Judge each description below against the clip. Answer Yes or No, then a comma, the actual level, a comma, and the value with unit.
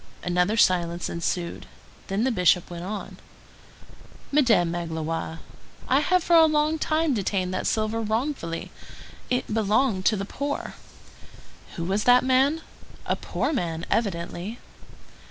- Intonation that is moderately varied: No, wide, 7.0 semitones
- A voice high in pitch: Yes, high, 210 Hz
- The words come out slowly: Yes, slow, 130 wpm